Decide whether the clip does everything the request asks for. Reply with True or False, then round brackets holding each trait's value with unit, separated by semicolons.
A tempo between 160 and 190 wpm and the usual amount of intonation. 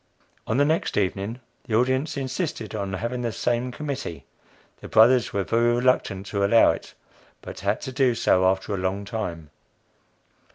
True (165 wpm; 4.4 semitones)